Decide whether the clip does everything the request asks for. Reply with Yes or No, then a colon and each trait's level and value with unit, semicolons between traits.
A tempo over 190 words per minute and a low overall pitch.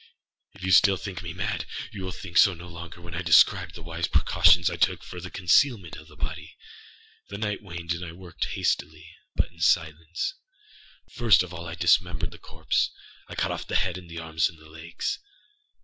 Yes: fast, 205 wpm; very low, 85 Hz